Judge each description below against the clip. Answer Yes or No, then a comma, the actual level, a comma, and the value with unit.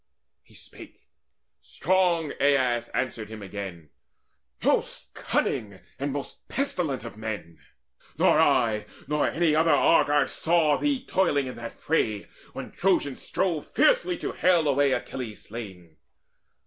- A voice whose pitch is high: No, medium, 140 Hz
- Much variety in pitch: Yes, wide, 7.3 semitones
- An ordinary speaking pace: No, slow, 125 wpm